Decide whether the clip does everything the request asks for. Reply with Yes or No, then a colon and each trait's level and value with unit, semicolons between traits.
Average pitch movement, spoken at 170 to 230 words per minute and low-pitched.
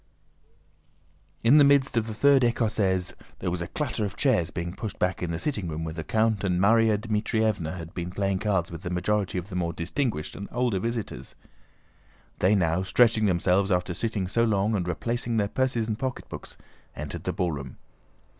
Yes: average, 4.3 semitones; average, 185 wpm; low, 100 Hz